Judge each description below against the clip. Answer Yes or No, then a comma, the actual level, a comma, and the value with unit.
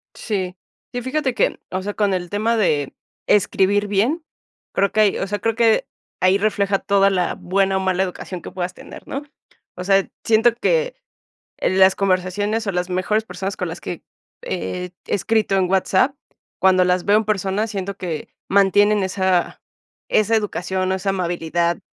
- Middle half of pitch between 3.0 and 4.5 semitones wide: No, narrow, 2.4 semitones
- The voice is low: No, high, 195 Hz